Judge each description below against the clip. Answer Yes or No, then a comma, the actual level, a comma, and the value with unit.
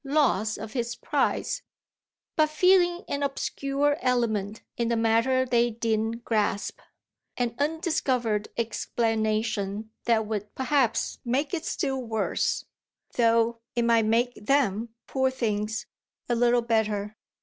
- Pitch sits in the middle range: No, high, 235 Hz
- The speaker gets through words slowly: Yes, slow, 120 wpm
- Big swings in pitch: No, average, 3.3 semitones